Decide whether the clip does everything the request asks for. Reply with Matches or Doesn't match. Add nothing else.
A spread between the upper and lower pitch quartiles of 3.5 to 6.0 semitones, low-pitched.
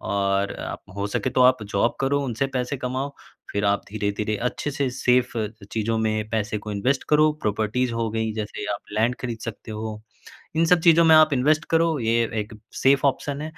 Matches